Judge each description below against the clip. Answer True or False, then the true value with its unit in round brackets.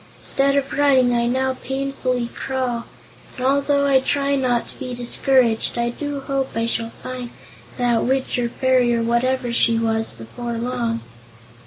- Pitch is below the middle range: False (250 Hz)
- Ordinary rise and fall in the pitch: False (2.2 semitones)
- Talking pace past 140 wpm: True (160 wpm)